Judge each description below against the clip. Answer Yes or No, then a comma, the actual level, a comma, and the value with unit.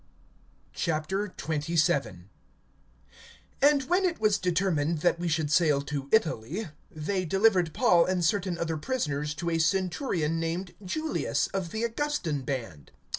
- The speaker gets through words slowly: Yes, slow, 125 wpm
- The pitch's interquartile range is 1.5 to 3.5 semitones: No, average, 4.5 semitones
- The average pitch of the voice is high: No, medium, 170 Hz